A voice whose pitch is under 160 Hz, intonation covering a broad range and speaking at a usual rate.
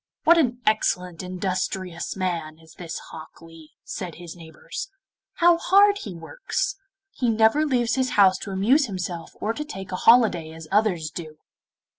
No: high, 190 Hz; wide, 6.6 semitones; average, 160 wpm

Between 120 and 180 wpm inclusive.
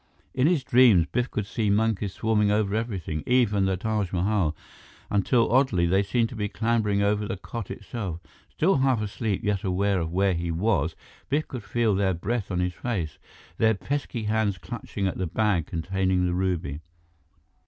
Yes: average, 175 wpm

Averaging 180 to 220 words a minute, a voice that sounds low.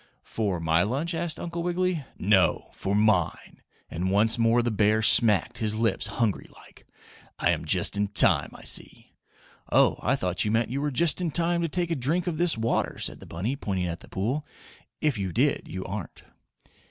Yes: average, 195 wpm; low, 115 Hz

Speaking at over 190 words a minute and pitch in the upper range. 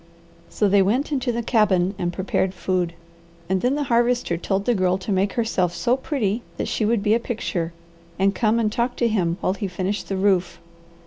Yes: fast, 205 wpm; high, 205 Hz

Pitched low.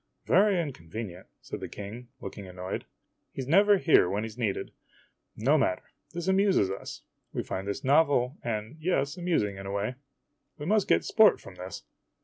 Yes: low, 120 Hz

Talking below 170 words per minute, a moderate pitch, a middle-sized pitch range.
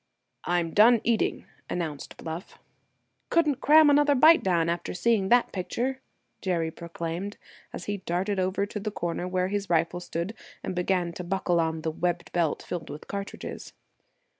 Yes: average, 160 wpm; medium, 180 Hz; average, 3.7 semitones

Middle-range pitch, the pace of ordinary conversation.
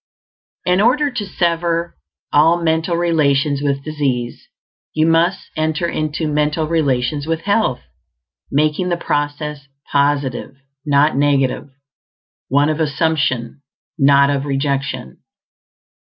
No: medium, 150 Hz; slow, 110 wpm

